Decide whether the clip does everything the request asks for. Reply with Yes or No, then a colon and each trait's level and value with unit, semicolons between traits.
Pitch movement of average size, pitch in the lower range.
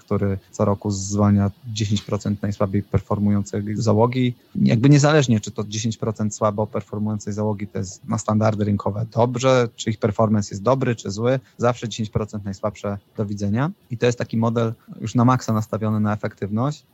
No: narrow, 2.2 semitones; low, 110 Hz